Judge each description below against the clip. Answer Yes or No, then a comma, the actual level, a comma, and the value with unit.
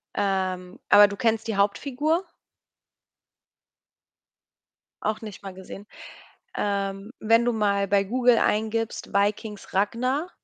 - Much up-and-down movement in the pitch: No, narrow, 2.5 semitones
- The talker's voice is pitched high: Yes, high, 210 Hz